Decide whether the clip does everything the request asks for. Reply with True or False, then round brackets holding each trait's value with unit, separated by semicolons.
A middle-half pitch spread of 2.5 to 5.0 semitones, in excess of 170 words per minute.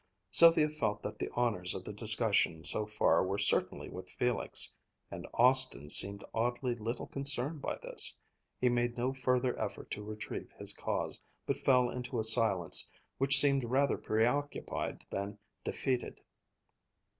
False (3.8 semitones; 145 wpm)